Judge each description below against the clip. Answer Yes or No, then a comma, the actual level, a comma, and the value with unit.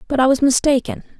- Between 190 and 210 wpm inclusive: Yes, average, 200 wpm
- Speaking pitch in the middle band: No, very high, 270 Hz